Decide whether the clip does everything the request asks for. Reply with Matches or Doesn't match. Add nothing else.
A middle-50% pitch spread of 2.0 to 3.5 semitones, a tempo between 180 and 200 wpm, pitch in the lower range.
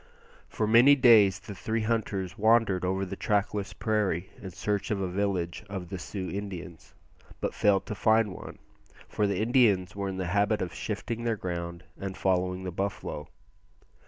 Doesn't match